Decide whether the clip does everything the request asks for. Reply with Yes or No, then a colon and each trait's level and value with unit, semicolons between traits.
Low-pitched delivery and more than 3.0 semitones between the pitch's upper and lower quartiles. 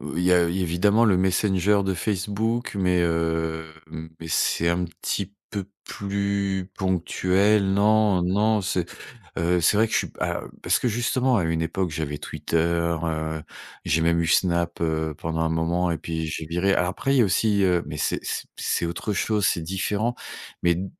Yes: very low, 90 Hz; average, 3.4 semitones